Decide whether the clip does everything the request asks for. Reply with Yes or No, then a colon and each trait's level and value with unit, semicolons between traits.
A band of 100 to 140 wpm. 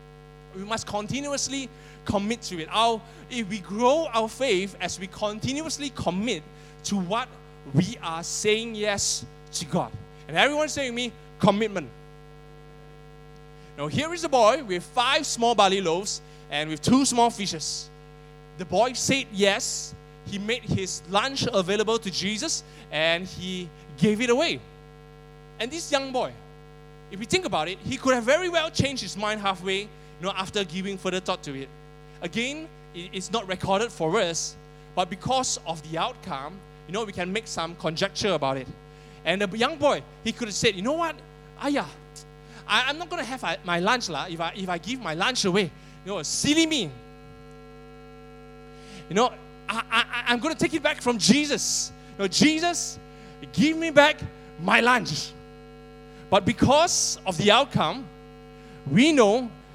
No: average, 165 wpm